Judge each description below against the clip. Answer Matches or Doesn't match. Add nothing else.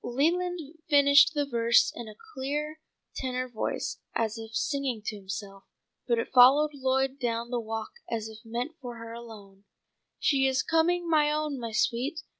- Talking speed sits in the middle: Matches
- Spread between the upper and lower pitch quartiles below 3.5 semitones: Doesn't match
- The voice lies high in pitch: Matches